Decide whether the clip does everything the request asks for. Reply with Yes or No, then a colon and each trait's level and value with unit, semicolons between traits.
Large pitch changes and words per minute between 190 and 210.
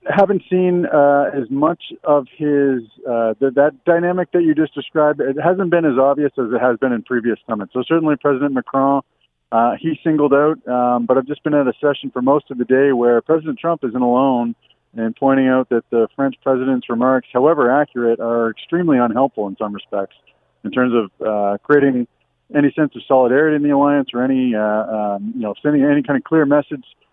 No: average, 3.4 semitones; fast, 205 wpm